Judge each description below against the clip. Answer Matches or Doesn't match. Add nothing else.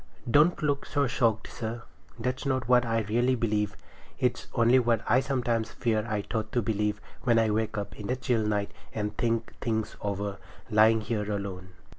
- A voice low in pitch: Matches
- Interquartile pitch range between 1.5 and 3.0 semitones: Matches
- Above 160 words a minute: Matches